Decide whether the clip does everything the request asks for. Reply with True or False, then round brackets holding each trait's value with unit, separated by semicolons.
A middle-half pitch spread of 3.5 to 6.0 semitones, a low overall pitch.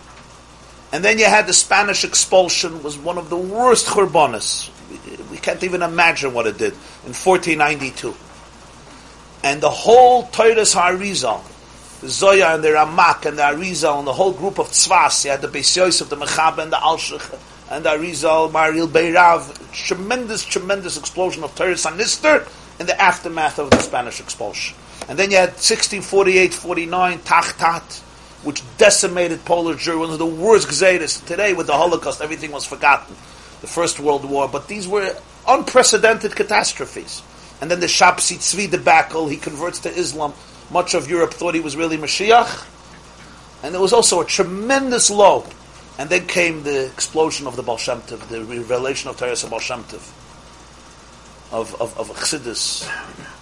False (4.2 semitones; 175 Hz)